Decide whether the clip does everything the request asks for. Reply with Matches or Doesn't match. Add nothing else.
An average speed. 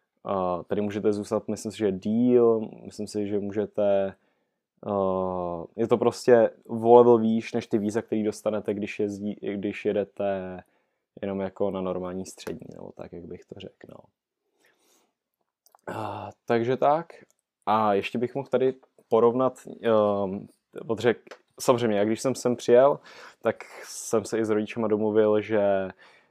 Matches